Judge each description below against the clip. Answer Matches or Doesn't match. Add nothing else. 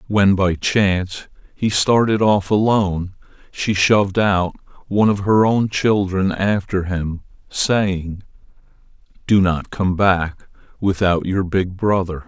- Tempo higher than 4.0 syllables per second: Doesn't match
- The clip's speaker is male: Matches